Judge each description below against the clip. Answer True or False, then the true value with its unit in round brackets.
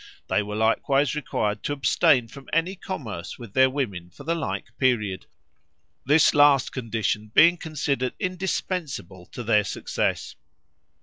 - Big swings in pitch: True (5.9 semitones)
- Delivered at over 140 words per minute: False (135 wpm)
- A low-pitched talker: True (130 Hz)